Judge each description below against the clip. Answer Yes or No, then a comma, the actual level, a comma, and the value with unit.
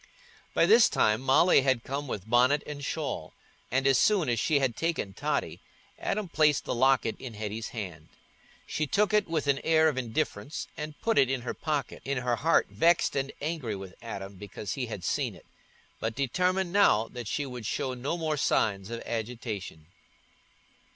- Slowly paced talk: No, average, 185 wpm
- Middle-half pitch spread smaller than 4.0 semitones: No, wide, 5.5 semitones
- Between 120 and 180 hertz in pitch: Yes, low, 135 Hz